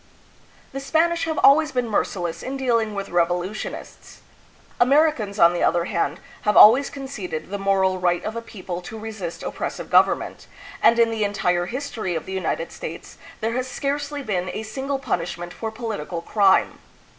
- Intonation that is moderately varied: No, wide, 6.3 semitones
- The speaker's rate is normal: Yes, average, 170 wpm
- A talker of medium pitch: No, high, 215 Hz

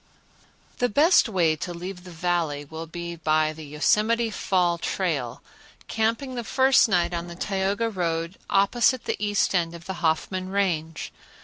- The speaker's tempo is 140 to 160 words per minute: Yes, average, 155 wpm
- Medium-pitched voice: Yes, medium, 180 Hz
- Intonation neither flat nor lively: Yes, average, 4.0 semitones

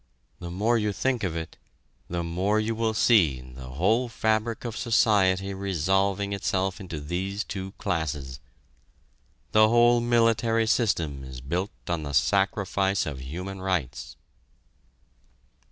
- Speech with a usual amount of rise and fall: Yes, average, 4.7 semitones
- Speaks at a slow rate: Yes, slow, 130 wpm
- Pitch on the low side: Yes, very low, 95 Hz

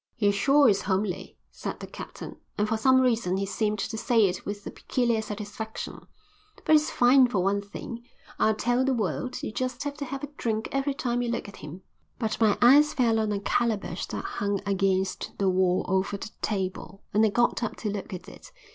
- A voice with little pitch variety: No, average, 3.6 semitones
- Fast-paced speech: Yes, fast, 210 wpm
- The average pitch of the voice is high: Yes, high, 215 Hz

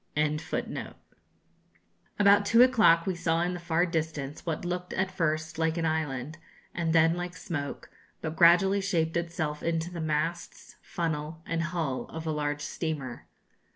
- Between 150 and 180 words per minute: Yes, average, 155 wpm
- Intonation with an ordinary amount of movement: No, narrow, 1.9 semitones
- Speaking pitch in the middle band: Yes, medium, 165 Hz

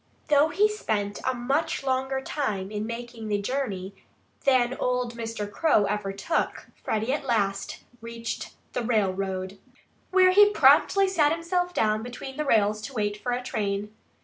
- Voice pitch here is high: Yes, high, 240 Hz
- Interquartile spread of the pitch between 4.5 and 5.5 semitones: Yes, average, 5.2 semitones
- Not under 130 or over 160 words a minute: Yes, average, 155 wpm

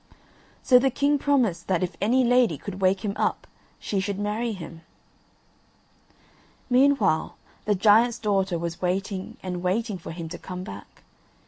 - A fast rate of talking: No, average, 150 wpm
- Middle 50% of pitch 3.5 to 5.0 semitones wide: Yes, average, 4.5 semitones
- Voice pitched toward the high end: Yes, high, 200 Hz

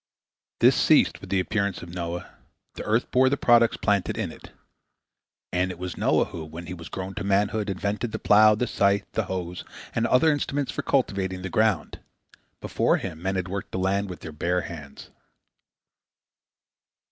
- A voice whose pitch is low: Yes, very low, 95 Hz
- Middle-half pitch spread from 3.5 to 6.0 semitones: No, average, 3.1 semitones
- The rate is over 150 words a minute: Yes, average, 180 wpm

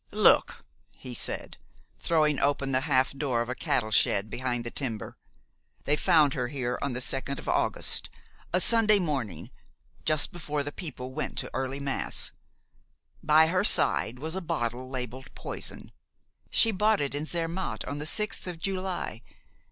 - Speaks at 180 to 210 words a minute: No, average, 160 wpm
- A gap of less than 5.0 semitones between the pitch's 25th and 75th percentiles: Yes, average, 4.5 semitones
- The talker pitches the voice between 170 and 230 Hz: No, medium, 140 Hz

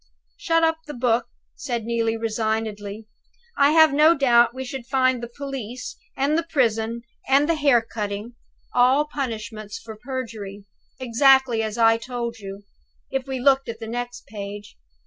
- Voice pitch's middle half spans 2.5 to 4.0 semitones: Yes, average, 3.2 semitones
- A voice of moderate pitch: No, high, 240 Hz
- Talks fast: No, average, 155 wpm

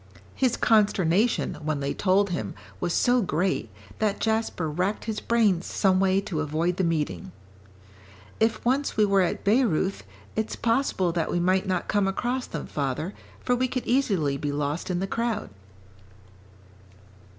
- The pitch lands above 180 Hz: Yes, high, 190 Hz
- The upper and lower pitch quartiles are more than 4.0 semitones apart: Yes, average, 5.0 semitones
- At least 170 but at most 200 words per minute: No, average, 155 wpm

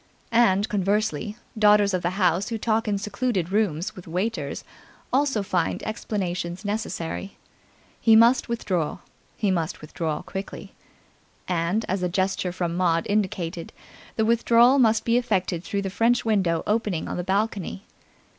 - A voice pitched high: Yes, high, 200 Hz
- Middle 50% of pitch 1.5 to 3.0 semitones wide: No, average, 3.6 semitones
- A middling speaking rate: Yes, average, 145 wpm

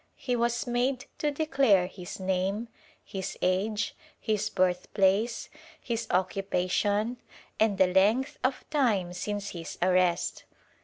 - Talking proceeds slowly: Yes, slow, 120 wpm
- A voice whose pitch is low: No, high, 205 Hz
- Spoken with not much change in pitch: No, average, 4.3 semitones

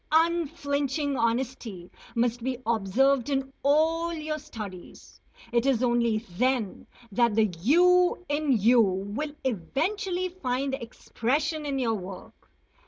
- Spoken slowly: Yes, slow, 115 wpm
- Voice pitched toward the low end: No, very high, 265 Hz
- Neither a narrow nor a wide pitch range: Yes, average, 4.9 semitones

